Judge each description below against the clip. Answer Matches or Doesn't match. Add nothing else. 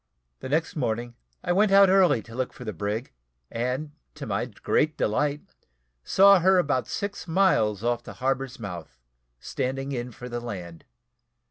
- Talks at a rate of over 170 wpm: Doesn't match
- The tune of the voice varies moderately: Doesn't match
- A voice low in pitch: Matches